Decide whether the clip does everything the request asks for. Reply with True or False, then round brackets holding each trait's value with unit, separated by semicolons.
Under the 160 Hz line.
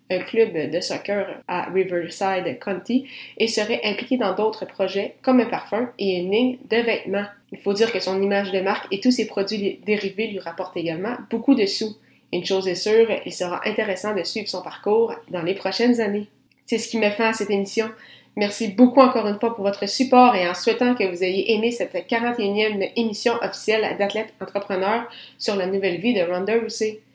False (210 Hz)